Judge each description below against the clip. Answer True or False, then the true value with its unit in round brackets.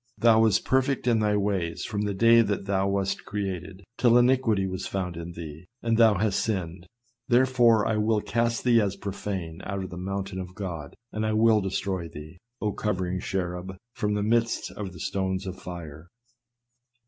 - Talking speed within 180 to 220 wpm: True (185 wpm)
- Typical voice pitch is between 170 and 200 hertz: False (100 Hz)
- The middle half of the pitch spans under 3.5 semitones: True (3.0 semitones)